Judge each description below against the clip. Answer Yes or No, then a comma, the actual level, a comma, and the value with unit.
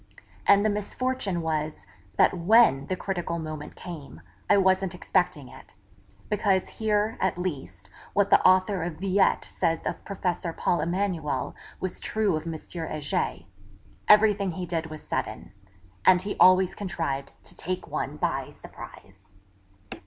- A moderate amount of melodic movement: Yes, average, 4.0 semitones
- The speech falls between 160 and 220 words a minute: No, average, 140 wpm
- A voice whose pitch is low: No, medium, 180 Hz